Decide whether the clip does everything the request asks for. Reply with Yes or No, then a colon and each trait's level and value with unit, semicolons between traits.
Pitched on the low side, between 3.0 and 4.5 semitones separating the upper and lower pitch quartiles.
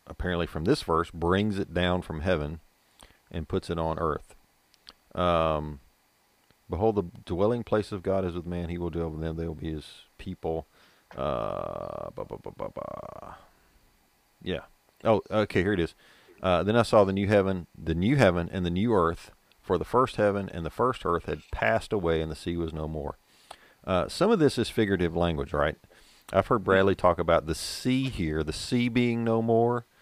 Yes: very low, 90 Hz; average, 4.2 semitones